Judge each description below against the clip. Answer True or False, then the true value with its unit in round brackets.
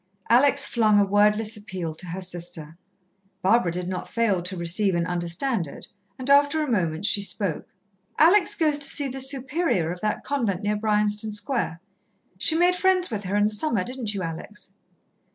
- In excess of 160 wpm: True (180 wpm)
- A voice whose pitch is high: True (210 Hz)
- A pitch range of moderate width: False (6.5 semitones)